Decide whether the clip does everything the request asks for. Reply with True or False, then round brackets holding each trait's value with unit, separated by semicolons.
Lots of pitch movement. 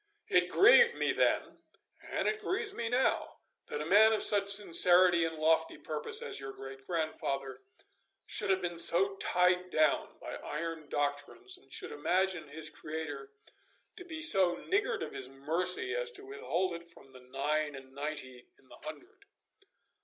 True (6.4 semitones)